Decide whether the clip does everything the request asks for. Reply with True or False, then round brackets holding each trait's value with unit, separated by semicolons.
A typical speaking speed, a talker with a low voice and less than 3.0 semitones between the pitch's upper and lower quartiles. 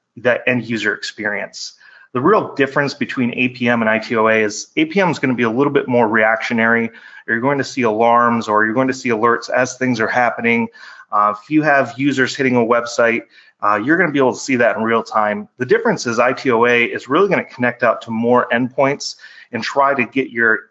False (215 wpm; 120 Hz; 2.5 semitones)